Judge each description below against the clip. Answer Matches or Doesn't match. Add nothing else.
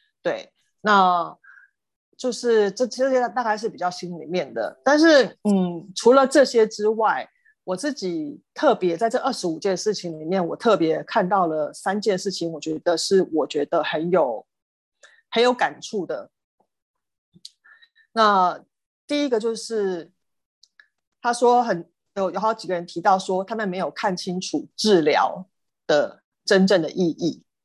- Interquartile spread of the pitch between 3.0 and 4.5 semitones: Doesn't match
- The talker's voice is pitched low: Doesn't match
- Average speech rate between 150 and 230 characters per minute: Matches